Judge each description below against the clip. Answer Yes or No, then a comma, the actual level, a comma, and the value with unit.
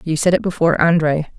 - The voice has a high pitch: No, medium, 165 Hz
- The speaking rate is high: Yes, fast, 215 wpm